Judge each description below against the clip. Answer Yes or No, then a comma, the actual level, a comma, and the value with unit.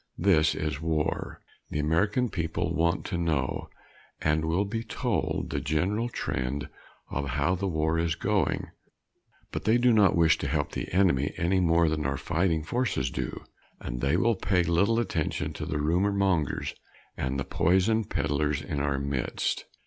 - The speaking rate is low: No, average, 165 wpm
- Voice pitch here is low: Yes, very low, 80 Hz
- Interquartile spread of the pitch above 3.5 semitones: Yes, average, 4.5 semitones